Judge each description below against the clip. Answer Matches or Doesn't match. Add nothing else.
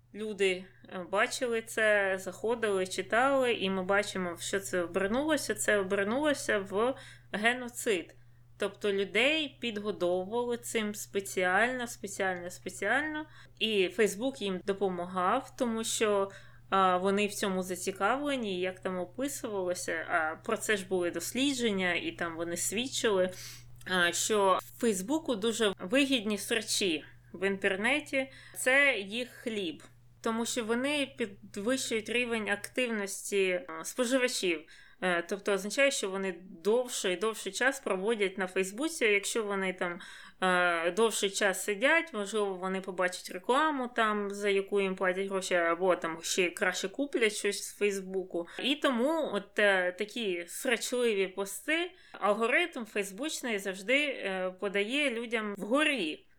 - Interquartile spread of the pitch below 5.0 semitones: Matches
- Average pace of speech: Matches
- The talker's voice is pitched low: Doesn't match